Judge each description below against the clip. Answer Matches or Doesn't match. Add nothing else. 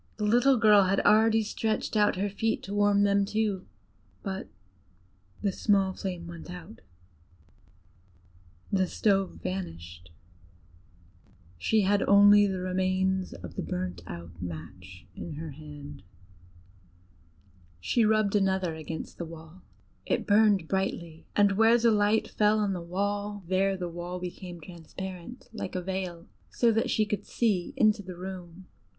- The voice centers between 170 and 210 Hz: Matches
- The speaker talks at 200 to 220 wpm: Doesn't match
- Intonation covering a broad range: Doesn't match